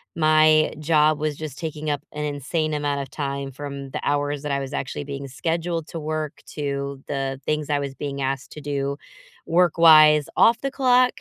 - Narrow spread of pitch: Yes, narrow, 1.9 semitones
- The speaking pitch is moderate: Yes, medium, 150 Hz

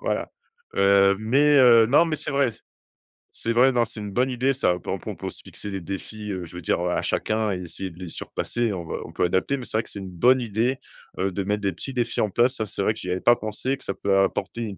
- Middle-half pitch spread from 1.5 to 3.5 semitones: No, average, 4.1 semitones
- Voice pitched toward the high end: No, low, 110 Hz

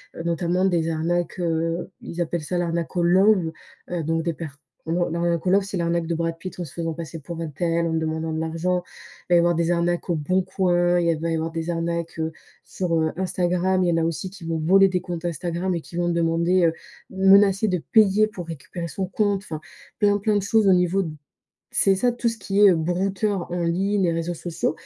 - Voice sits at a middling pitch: Yes, medium, 175 Hz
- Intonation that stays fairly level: Yes, narrow, 2.2 semitones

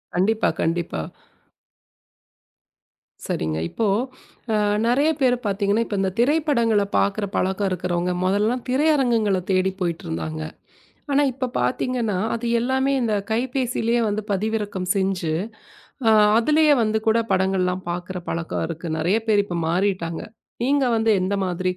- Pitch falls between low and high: No, high, 205 Hz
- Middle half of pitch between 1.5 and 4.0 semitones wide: No, average, 4.5 semitones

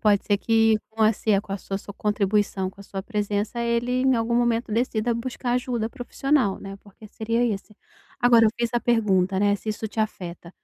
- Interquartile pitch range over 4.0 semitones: No, average, 2.8 semitones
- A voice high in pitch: Yes, high, 220 Hz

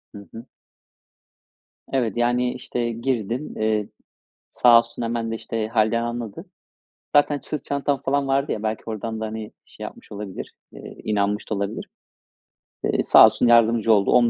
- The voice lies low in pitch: Yes, low, 115 Hz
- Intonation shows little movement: Yes, narrow, 2.0 semitones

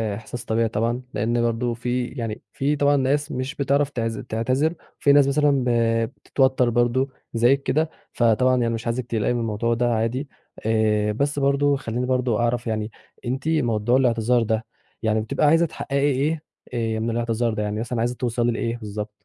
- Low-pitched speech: Yes, low, 120 Hz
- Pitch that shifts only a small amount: No, average, 3.0 semitones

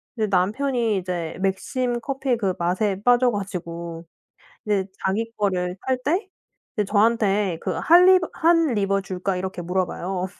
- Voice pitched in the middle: No, high, 200 Hz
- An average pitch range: Yes, average, 4.8 semitones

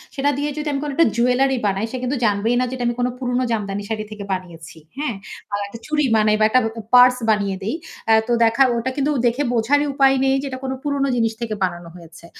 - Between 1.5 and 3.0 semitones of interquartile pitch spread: No, average, 4.2 semitones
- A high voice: Yes, high, 240 Hz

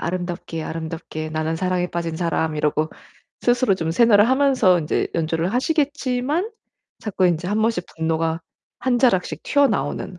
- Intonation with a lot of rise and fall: Yes, wide, 7.0 semitones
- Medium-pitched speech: Yes, medium, 180 Hz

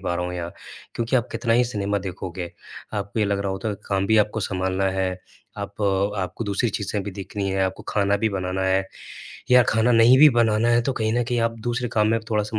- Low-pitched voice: Yes, low, 105 Hz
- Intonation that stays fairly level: No, average, 3.0 semitones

